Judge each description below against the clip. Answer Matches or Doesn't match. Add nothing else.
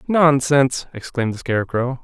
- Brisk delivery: Doesn't match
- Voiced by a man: Matches